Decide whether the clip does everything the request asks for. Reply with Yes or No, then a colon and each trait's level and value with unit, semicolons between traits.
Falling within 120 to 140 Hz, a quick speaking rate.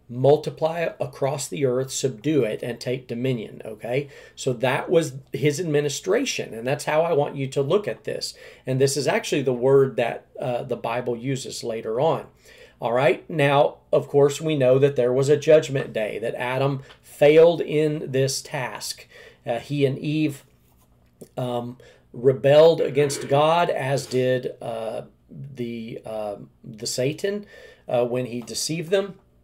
No: low, 135 Hz; average, 155 wpm